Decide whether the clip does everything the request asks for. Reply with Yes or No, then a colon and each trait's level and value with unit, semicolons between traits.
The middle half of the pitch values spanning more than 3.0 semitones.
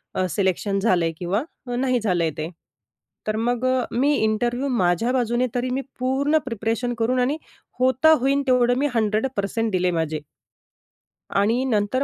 Yes: average, 4.2 semitones